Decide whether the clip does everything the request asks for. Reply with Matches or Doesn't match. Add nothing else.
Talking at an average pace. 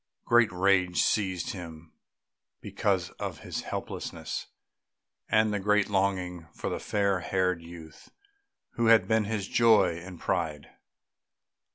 Doesn't match